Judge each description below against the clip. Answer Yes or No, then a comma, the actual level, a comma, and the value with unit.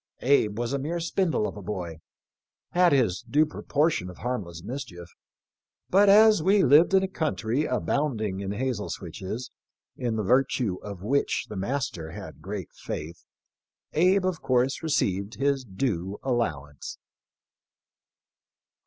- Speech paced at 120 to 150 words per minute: Yes, average, 140 wpm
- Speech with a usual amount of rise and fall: No, wide, 7.4 semitones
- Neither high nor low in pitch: No, low, 120 Hz